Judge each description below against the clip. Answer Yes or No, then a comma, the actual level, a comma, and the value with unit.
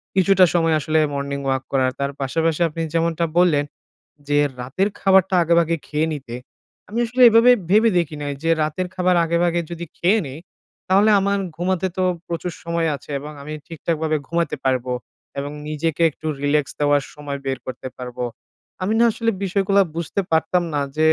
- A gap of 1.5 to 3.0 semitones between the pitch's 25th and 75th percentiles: No, average, 4.0 semitones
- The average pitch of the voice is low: No, medium, 165 Hz